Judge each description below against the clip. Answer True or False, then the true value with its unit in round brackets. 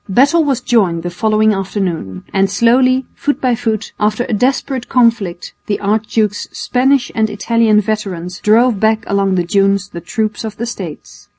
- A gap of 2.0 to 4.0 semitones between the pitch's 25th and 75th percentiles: True (3.4 semitones)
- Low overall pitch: False (215 Hz)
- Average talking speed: True (165 wpm)